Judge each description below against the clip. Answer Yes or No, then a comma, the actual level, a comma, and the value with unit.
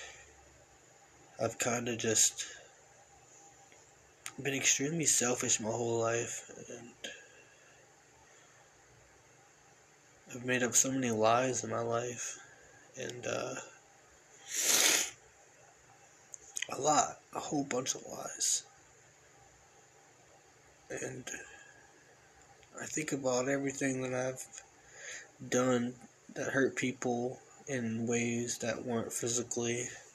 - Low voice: Yes, low, 125 Hz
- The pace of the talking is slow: Yes, slow, 90 wpm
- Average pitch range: No, narrow, 2.0 semitones